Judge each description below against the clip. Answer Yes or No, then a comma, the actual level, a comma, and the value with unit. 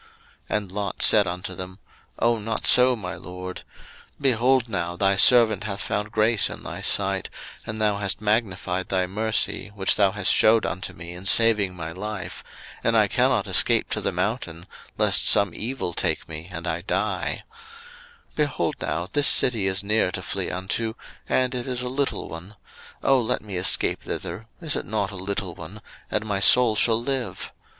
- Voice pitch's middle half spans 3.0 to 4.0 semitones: Yes, average, 3.7 semitones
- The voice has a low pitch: Yes, low, 105 Hz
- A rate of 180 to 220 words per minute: Yes, average, 185 wpm